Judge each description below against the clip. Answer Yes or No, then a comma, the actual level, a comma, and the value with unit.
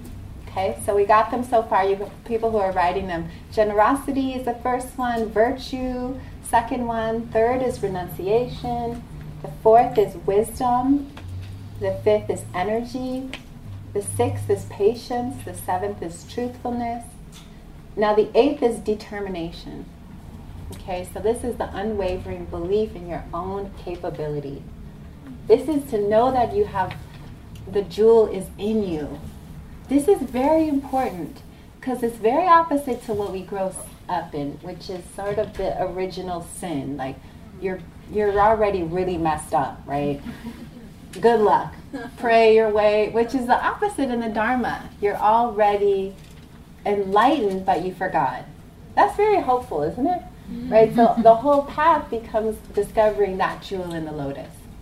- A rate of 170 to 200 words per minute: No, average, 145 wpm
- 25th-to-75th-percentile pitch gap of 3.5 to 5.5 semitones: Yes, average, 5.0 semitones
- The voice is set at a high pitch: Yes, high, 215 Hz